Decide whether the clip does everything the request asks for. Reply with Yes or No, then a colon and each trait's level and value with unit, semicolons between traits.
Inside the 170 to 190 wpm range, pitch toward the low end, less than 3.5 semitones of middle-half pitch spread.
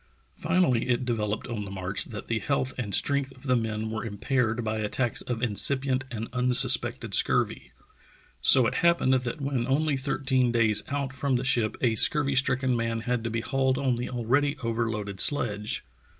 Yes: average, 180 wpm; low, 125 Hz; average, 3.1 semitones